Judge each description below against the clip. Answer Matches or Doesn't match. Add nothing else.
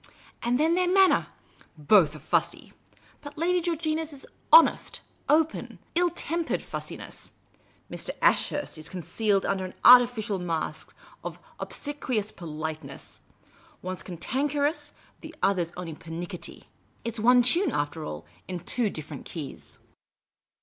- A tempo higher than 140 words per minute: Doesn't match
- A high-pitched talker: Matches